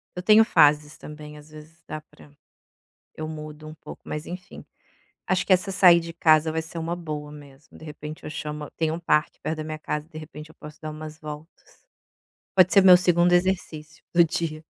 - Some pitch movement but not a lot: No, narrow, 2.1 semitones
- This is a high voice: No, medium, 155 Hz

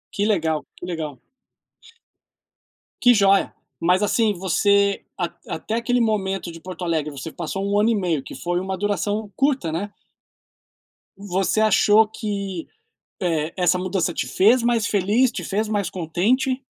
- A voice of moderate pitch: No, high, 195 Hz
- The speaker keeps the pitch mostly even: No, average, 3.5 semitones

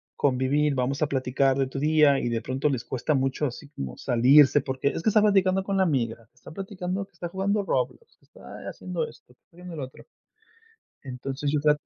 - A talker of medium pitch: Yes, medium, 145 Hz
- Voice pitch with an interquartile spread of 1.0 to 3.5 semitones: No, wide, 5.4 semitones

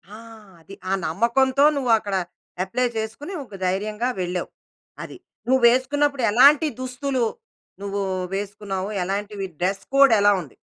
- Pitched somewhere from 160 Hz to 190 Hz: No, high, 220 Hz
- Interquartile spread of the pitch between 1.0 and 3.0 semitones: No, average, 4.9 semitones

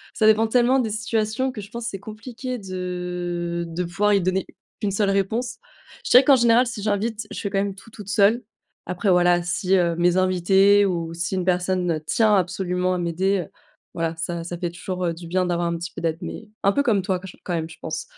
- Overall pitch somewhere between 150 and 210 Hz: Yes, high, 190 Hz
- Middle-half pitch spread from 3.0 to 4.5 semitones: Yes, average, 3.4 semitones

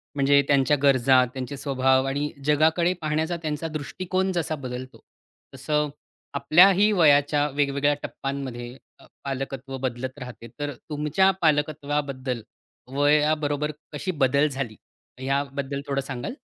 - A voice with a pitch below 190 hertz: Yes, medium, 140 Hz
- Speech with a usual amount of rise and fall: No, narrow, 2.1 semitones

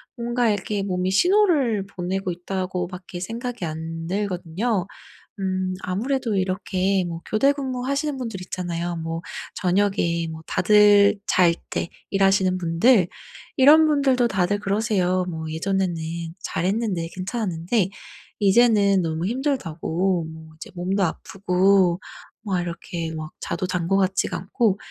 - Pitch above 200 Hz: No, high, 190 Hz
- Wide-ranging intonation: No, average, 3.5 semitones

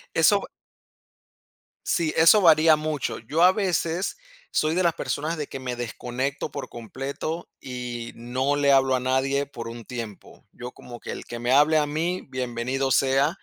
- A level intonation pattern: No, average, 4.1 semitones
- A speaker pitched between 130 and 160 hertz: Yes, low, 135 Hz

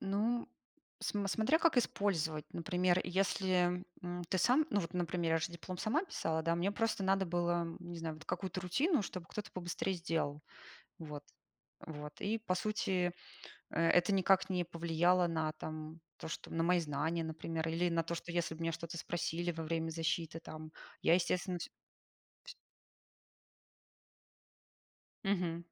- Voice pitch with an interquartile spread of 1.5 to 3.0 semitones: Yes, narrow, 2.5 semitones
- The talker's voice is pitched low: No, medium, 175 Hz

